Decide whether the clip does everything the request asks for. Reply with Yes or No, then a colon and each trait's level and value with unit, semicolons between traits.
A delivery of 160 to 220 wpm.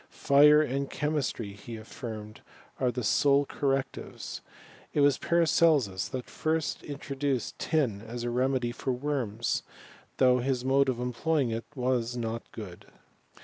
No: slow, 135 wpm